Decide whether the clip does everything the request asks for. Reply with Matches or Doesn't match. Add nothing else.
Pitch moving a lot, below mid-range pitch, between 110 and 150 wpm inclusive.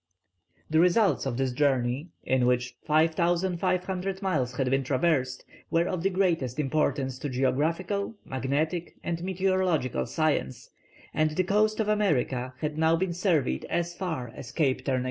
Doesn't match